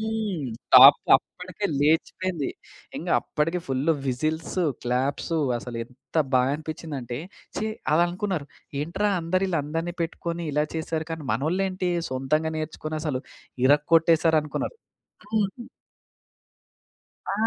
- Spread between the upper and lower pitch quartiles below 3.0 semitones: No, average, 3.3 semitones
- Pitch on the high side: No, medium, 160 Hz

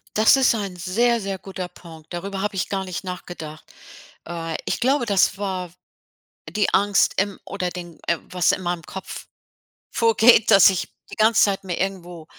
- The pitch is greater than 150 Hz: Yes, high, 190 Hz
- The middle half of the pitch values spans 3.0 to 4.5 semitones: No, narrow, 2.6 semitones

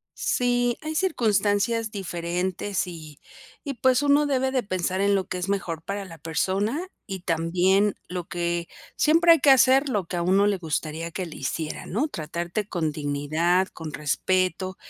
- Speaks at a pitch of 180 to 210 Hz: Yes, high, 190 Hz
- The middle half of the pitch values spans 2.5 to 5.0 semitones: No, wide, 5.4 semitones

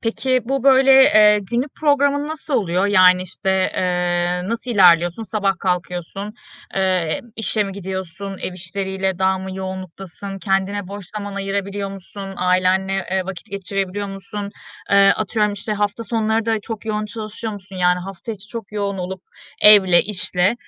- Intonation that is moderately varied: No, narrow, 2.3 semitones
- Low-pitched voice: No, high, 195 Hz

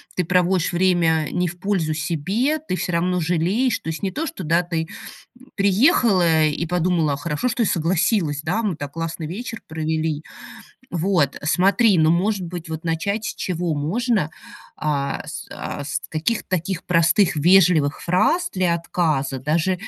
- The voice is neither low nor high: Yes, medium, 170 Hz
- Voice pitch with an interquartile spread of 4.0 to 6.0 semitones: No, average, 3.2 semitones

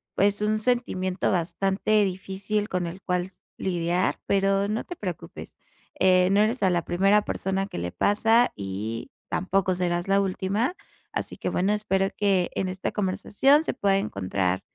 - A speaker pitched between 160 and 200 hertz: Yes, high, 190 Hz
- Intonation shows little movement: Yes, narrow, 2.3 semitones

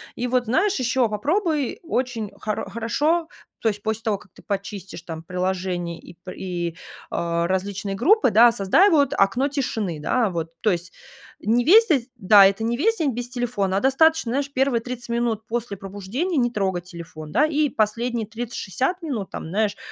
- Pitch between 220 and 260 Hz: Yes, high, 225 Hz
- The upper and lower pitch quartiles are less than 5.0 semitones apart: No, average, 5.3 semitones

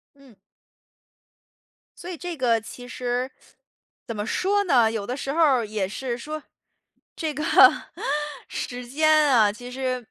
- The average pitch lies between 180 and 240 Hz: No, very high, 255 Hz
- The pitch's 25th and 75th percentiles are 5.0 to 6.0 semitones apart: No, average, 4.4 semitones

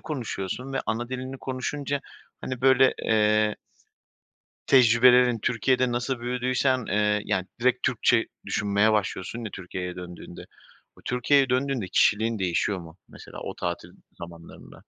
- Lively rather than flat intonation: No, average, 4.1 semitones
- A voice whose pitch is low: Yes, low, 120 Hz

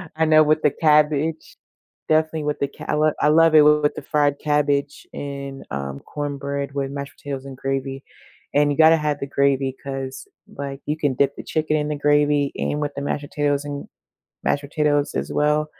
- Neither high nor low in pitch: Yes, medium, 145 Hz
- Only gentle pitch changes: Yes, narrow, 1.4 semitones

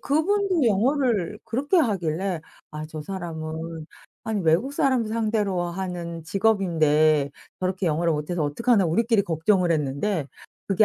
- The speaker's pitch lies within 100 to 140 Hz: No, medium, 185 Hz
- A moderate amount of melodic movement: No, wide, 5.7 semitones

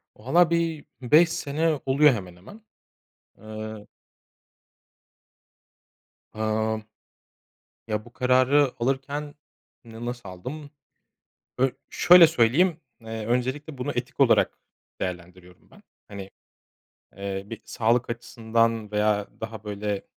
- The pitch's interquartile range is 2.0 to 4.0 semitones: No, average, 5.0 semitones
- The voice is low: Yes, low, 115 Hz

